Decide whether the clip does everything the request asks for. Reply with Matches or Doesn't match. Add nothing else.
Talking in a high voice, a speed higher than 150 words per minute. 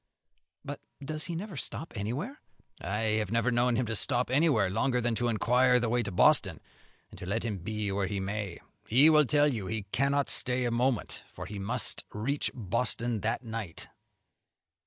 Doesn't match